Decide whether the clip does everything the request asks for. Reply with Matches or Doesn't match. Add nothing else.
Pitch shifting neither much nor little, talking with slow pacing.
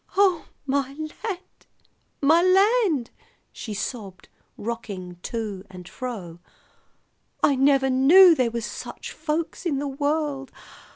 Doesn't match